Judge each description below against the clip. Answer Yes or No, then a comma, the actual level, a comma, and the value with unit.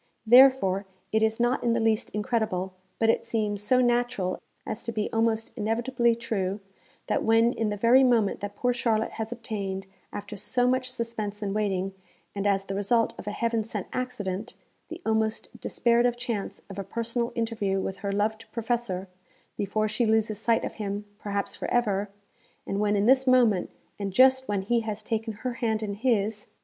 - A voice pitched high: Yes, high, 220 Hz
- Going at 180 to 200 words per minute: Yes, average, 185 wpm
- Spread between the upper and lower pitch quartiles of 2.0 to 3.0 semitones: Yes, narrow, 2.6 semitones